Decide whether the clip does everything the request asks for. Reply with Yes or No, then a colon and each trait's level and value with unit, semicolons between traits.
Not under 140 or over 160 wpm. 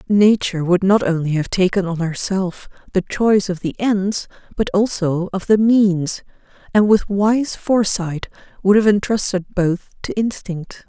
Yes: average, 155 wpm